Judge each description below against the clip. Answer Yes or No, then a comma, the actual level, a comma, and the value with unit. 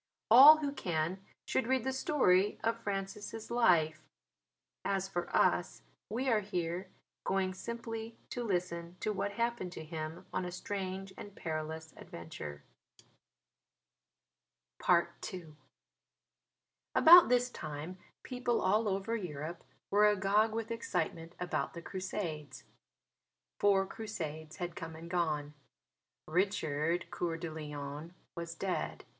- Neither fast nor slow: No, slow, 120 wpm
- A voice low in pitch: No, medium, 185 Hz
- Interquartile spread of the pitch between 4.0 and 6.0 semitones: Yes, average, 4.8 semitones